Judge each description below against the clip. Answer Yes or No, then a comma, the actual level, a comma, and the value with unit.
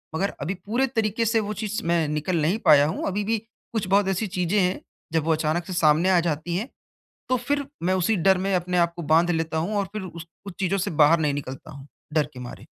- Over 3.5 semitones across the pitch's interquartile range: Yes, average, 4.1 semitones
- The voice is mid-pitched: Yes, medium, 180 Hz